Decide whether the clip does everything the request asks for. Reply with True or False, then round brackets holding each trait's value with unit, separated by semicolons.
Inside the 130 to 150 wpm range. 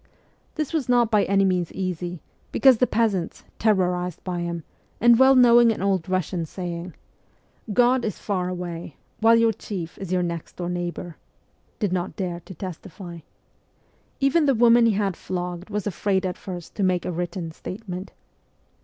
False (170 wpm)